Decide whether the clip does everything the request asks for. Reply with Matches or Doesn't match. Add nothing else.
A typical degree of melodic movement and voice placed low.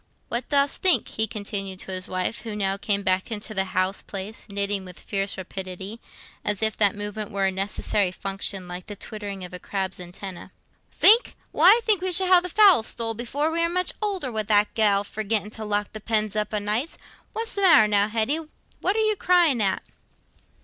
Doesn't match